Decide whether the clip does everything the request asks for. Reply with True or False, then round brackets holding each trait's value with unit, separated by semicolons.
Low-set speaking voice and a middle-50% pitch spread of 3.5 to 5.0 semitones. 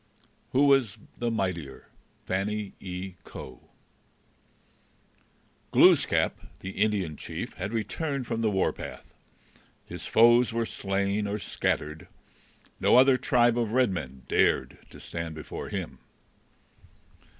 True (105 Hz; 4.3 semitones)